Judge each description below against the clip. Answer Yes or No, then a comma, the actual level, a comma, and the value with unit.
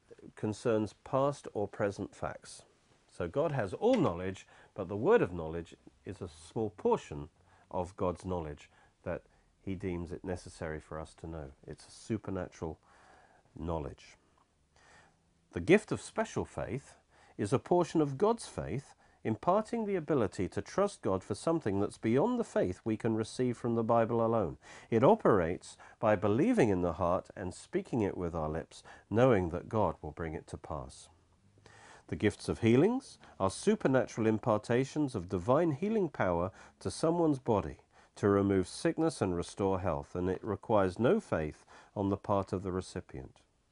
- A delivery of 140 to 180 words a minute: Yes, average, 160 wpm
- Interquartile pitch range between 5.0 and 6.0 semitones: Yes, wide, 5.4 semitones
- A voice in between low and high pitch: No, low, 100 Hz